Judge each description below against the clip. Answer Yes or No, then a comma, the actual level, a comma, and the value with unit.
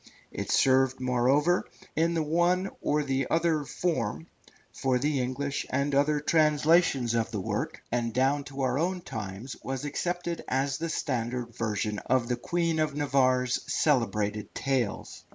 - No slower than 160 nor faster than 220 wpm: No, average, 150 wpm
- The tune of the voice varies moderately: Yes, average, 3.9 semitones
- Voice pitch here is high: No, low, 135 Hz